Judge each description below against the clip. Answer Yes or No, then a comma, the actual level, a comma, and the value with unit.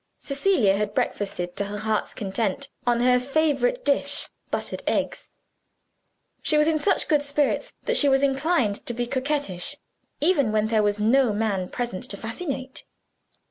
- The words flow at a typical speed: Yes, average, 155 wpm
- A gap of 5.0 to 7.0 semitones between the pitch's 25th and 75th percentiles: Yes, wide, 5.4 semitones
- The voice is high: Yes, very high, 250 Hz